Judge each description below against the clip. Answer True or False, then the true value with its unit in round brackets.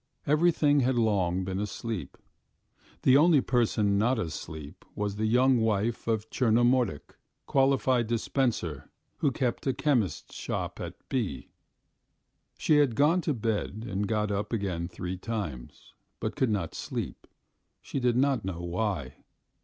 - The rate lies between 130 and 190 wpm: True (140 wpm)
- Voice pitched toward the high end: False (110 Hz)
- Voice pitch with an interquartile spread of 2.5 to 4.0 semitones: False (5.2 semitones)